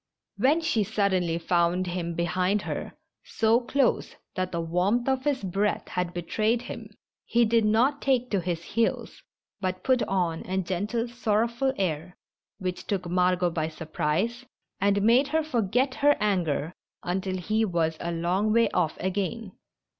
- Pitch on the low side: No, high, 195 Hz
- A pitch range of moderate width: Yes, average, 4.7 semitones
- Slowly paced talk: No, average, 155 wpm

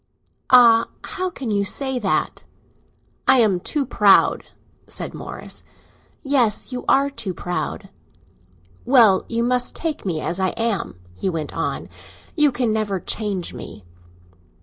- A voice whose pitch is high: Yes, high, 225 Hz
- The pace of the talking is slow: Yes, slow, 130 wpm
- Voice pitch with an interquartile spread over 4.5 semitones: Yes, average, 5.1 semitones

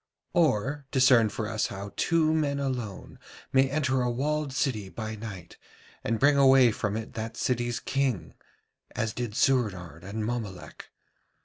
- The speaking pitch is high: No, low, 120 Hz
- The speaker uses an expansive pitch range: No, average, 4.1 semitones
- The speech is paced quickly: No, average, 145 wpm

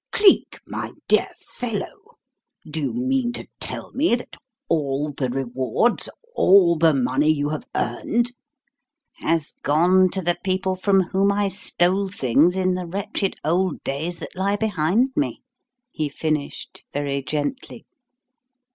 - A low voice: No, medium, 180 Hz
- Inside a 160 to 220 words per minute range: No, average, 140 wpm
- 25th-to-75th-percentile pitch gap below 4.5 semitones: No, average, 5.1 semitones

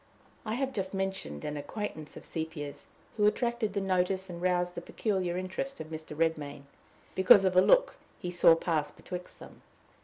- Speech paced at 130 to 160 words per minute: No, average, 175 wpm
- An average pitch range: Yes, average, 3.5 semitones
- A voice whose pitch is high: No, medium, 180 Hz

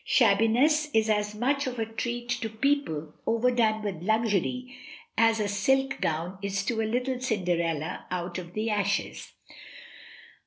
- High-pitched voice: Yes, high, 220 Hz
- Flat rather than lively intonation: No, average, 4.0 semitones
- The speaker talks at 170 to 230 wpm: No, average, 145 wpm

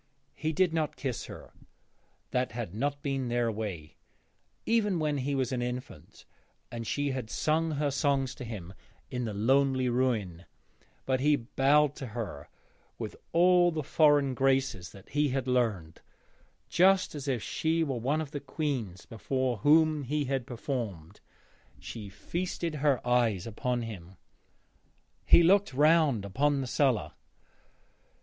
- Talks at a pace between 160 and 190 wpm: No, average, 145 wpm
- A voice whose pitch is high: No, low, 130 Hz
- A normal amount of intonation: Yes, average, 4.3 semitones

